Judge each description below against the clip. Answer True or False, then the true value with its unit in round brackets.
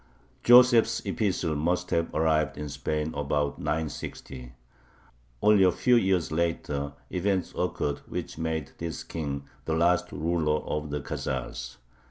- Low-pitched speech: True (80 Hz)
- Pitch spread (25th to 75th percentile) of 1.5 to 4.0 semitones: True (3.5 semitones)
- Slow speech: True (130 wpm)